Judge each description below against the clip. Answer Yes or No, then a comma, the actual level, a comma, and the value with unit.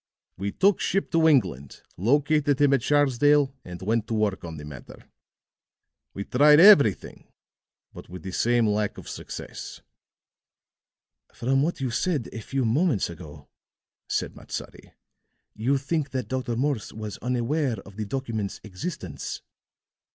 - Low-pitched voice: Yes, low, 120 Hz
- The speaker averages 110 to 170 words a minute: Yes, average, 140 wpm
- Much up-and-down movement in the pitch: Yes, wide, 6.0 semitones